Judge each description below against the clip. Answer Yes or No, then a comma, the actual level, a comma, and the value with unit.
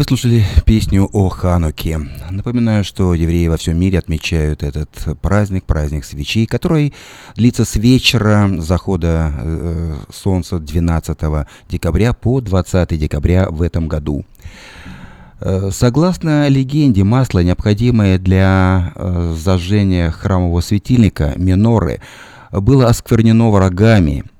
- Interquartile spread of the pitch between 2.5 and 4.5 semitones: No, average, 5.0 semitones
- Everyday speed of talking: No, slow, 105 wpm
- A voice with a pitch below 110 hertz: Yes, very low, 95 Hz